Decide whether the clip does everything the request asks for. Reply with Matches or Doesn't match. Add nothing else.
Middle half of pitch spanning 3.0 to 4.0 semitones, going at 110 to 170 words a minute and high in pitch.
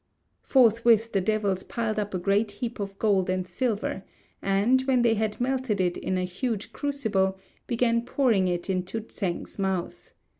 Matches